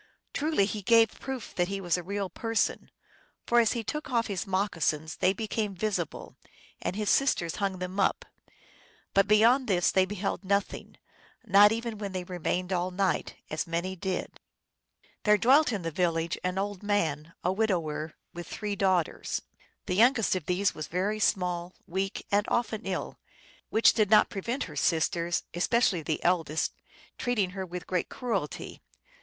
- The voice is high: Yes, high, 195 Hz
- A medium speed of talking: Yes, average, 165 wpm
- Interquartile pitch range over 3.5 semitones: No, average, 3.2 semitones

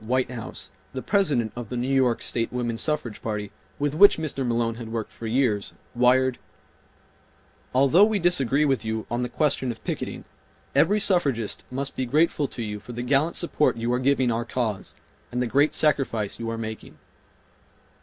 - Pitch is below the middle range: Yes, low, 125 Hz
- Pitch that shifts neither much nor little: Yes, average, 3.5 semitones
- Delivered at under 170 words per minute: No, average, 175 wpm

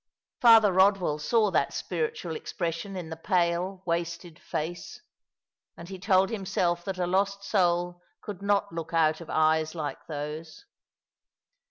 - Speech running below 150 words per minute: Yes, average, 140 wpm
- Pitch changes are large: No, average, 2.9 semitones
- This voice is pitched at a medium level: Yes, medium, 175 Hz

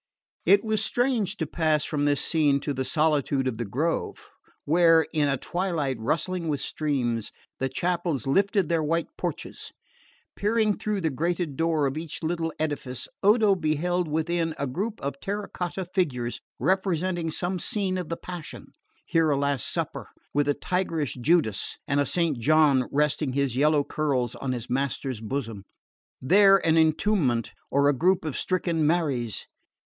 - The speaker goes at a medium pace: Yes, average, 160 wpm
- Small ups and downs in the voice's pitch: No, average, 4.2 semitones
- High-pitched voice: No, medium, 155 Hz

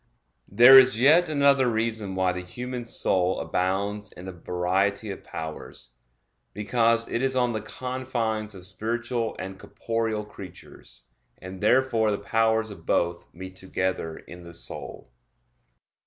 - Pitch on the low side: Yes, low, 105 Hz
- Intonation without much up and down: No, average, 4.3 semitones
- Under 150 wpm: Yes, average, 140 wpm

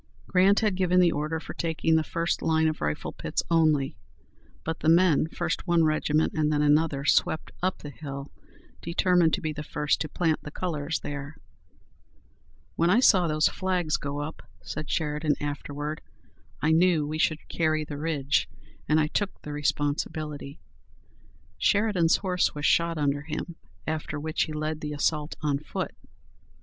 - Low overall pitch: No, medium, 155 Hz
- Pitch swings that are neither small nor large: No, narrow, 2.2 semitones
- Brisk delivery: No, average, 165 wpm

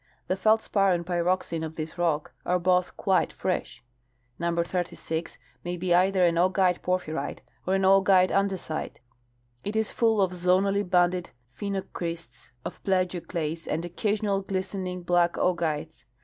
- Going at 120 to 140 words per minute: Yes, slow, 135 wpm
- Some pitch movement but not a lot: No, narrow, 2.0 semitones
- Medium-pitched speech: Yes, medium, 180 Hz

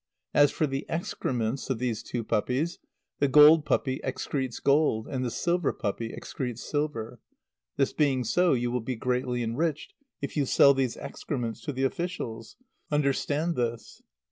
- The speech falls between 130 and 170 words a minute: Yes, average, 155 wpm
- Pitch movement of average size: Yes, average, 3.6 semitones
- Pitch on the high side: No, low, 130 Hz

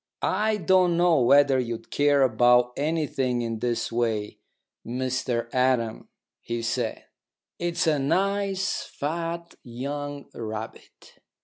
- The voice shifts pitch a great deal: Yes, wide, 5.8 semitones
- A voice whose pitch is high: No, low, 135 Hz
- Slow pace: Yes, slow, 110 wpm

